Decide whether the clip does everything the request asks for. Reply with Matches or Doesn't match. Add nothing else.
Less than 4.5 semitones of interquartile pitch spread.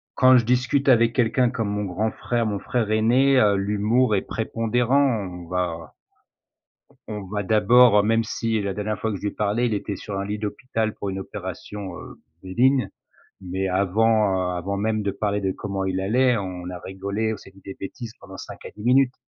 Matches